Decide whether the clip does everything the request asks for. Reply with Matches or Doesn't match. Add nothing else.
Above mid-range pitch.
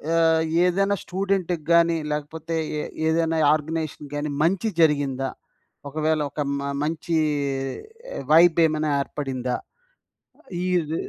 Doesn't match